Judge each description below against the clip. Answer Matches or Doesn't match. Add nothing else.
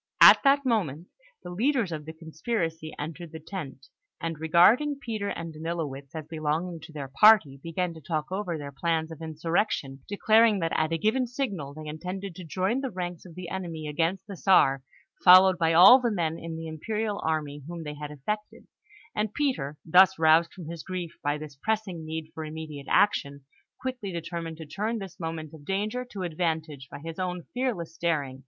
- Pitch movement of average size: Matches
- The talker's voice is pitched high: Doesn't match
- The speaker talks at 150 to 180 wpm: Doesn't match